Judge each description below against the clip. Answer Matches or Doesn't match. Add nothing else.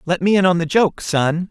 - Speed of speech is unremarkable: Doesn't match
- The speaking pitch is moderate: Matches